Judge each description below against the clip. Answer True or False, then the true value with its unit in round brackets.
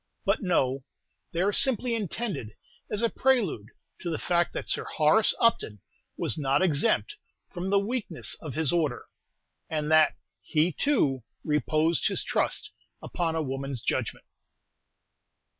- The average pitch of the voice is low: False (165 Hz)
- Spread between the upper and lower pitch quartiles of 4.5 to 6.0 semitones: True (5.5 semitones)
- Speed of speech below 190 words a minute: True (140 wpm)